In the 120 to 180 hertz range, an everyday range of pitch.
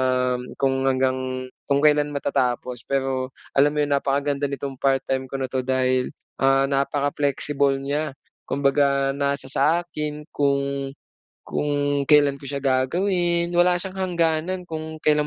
No: medium, 140 Hz; narrow, 1.8 semitones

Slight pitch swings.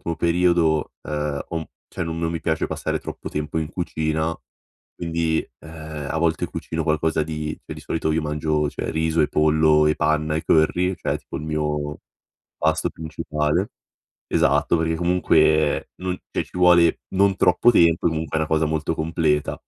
Yes: narrow, 1.3 semitones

